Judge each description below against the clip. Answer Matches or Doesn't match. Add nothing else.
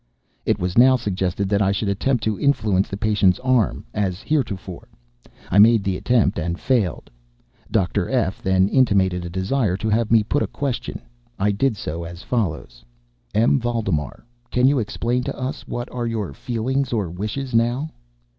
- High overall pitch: Doesn't match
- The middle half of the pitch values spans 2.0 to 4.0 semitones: Doesn't match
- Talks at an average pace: Matches